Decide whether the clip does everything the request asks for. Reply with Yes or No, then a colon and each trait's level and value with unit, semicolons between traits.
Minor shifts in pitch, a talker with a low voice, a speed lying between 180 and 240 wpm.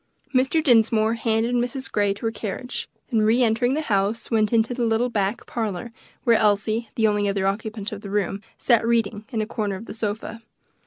No: narrow, 2.2 semitones; high, 225 Hz; average, 200 wpm